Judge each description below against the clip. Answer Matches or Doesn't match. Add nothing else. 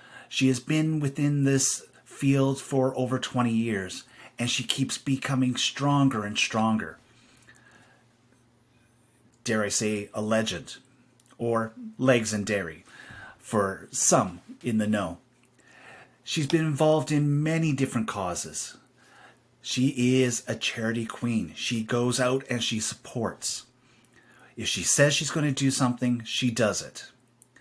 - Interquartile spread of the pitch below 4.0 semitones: Matches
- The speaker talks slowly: Matches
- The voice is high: Doesn't match